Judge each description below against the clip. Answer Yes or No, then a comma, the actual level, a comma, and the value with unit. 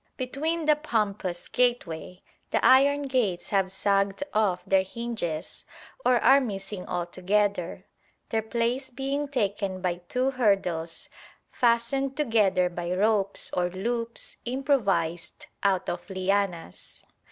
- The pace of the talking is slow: Yes, slow, 115 wpm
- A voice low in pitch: No, high, 205 Hz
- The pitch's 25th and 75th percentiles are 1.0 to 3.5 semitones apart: No, average, 5.3 semitones